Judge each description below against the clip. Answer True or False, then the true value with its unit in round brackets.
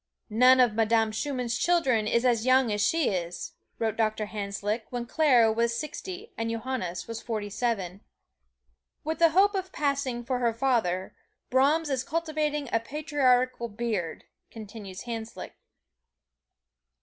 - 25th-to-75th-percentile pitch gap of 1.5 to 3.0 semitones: False (4.3 semitones)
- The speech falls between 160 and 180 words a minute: False (135 wpm)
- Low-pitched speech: False (235 Hz)